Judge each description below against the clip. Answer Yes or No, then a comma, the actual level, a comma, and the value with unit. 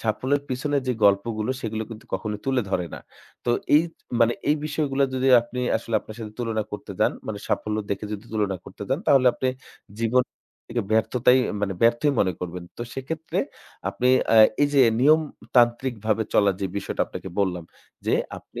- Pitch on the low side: Yes, low, 115 Hz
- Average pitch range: Yes, average, 3.5 semitones